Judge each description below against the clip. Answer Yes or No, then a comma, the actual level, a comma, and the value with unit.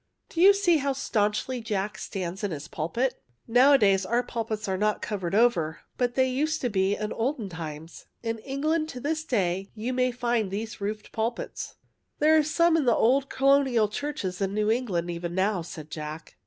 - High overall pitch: Yes, high, 225 Hz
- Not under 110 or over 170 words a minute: No, average, 195 wpm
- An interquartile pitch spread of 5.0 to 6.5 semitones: Yes, wide, 5.5 semitones